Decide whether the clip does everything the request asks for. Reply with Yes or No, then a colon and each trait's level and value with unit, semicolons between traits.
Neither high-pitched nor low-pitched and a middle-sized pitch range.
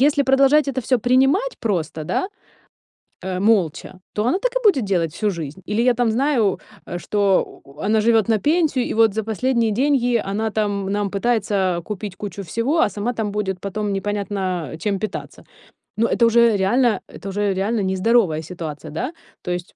No: high, 215 Hz; average, 4.0 semitones